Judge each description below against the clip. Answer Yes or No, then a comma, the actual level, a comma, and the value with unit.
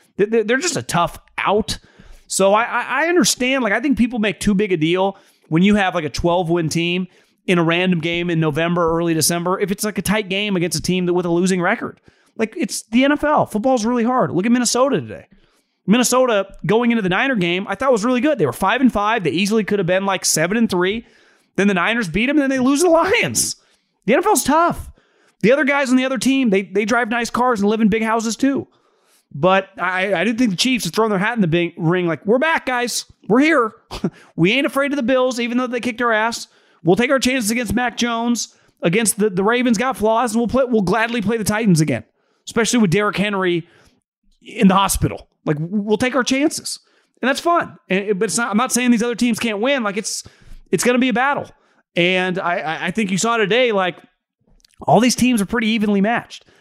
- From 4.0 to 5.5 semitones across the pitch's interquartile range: Yes, average, 4.7 semitones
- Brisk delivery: Yes, fast, 230 wpm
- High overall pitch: Yes, high, 220 Hz